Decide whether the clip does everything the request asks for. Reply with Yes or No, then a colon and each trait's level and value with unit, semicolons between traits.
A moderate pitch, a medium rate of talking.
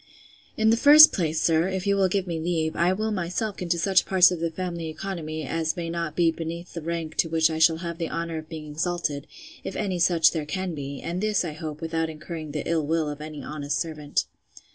No: medium, 165 Hz; fast, 235 wpm